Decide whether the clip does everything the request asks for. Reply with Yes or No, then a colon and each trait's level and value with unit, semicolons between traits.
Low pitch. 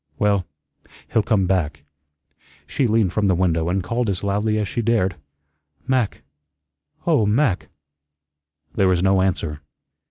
Yes: low, 100 Hz